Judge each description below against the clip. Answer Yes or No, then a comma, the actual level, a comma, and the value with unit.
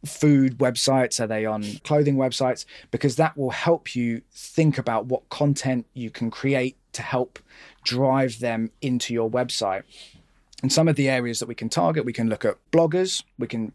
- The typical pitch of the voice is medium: No, low, 130 Hz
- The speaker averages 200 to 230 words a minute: No, average, 185 wpm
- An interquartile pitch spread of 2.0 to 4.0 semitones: Yes, average, 3.2 semitones